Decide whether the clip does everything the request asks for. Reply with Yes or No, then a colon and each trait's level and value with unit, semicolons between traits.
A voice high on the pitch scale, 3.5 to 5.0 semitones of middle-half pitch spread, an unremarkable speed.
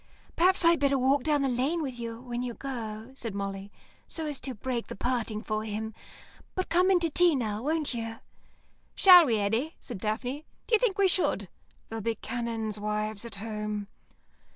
No: high, 240 Hz; wide, 5.4 semitones; average, 185 wpm